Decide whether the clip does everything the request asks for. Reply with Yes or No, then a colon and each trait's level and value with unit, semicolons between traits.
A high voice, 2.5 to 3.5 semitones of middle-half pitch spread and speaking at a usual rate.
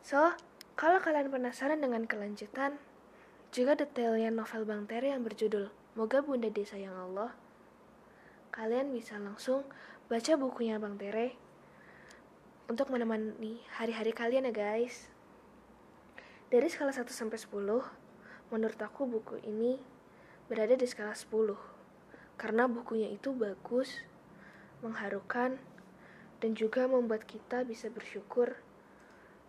Yes: high, 230 Hz; average, 3.1 semitones; average, 110 wpm